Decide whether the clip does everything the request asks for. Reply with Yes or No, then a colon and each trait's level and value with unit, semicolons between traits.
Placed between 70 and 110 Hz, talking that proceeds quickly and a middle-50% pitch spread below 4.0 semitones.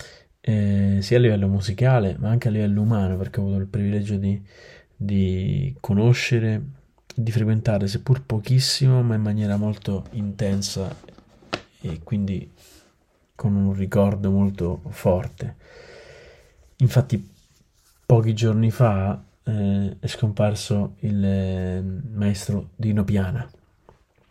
No: low, 105 Hz; slow, 115 wpm; average, 3.0 semitones